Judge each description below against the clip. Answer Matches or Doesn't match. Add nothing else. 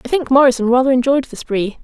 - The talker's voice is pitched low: Doesn't match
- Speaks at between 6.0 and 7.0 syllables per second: Matches